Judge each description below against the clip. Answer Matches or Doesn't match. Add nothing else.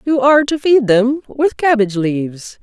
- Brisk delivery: Doesn't match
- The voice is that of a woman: Matches